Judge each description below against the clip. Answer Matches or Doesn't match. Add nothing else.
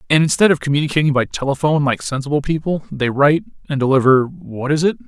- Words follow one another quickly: Doesn't match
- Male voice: Matches